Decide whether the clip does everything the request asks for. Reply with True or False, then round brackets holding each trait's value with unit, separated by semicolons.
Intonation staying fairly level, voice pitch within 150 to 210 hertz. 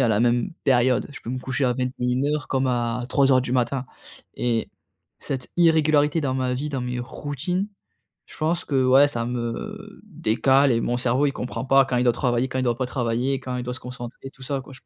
False (2.2 semitones; 130 Hz)